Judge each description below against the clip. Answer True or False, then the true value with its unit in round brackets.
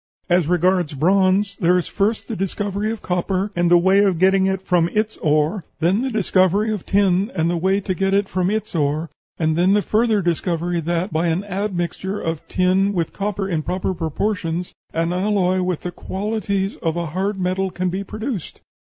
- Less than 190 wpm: False (195 wpm)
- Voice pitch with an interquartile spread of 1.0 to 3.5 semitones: True (2.5 semitones)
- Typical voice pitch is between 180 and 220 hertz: True (185 Hz)